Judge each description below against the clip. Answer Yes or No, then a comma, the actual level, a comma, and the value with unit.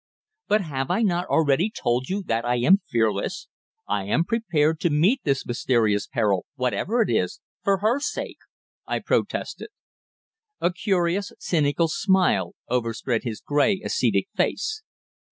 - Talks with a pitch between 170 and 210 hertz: No, medium, 155 Hz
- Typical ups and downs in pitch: No, wide, 8.2 semitones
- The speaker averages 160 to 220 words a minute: No, average, 140 wpm